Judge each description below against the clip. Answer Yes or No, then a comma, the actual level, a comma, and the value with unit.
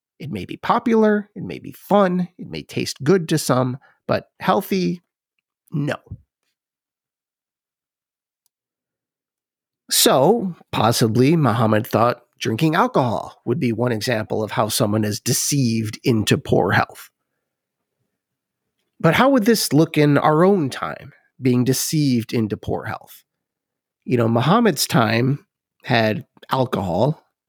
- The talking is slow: Yes, slow, 120 wpm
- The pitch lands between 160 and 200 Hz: No, low, 130 Hz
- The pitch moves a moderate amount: No, wide, 7.0 semitones